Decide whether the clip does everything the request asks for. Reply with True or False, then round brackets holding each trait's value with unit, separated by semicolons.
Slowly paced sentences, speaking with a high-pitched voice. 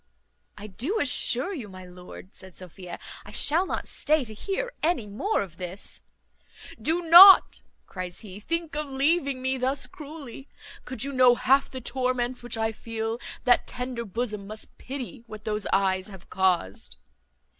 False (160 wpm; 240 Hz)